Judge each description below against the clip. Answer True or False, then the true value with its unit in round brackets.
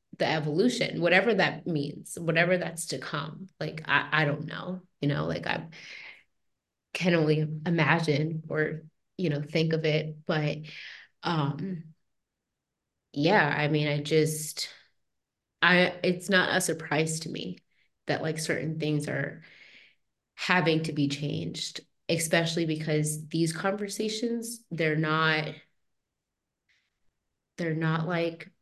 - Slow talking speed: True (125 wpm)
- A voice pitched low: False (160 Hz)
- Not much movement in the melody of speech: True (2.1 semitones)